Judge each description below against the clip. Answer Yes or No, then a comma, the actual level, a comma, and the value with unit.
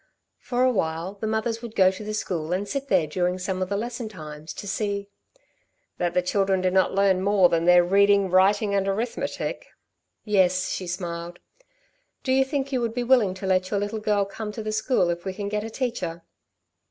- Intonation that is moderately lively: Yes, average, 3.0 semitones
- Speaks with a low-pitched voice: No, high, 200 Hz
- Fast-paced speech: Yes, fast, 215 wpm